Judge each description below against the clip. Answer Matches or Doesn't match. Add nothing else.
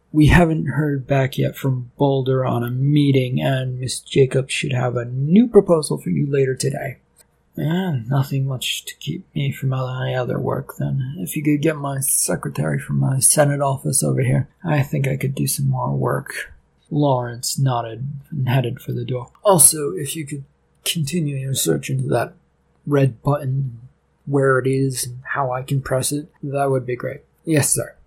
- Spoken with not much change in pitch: Matches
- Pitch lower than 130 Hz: Doesn't match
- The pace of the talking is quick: Doesn't match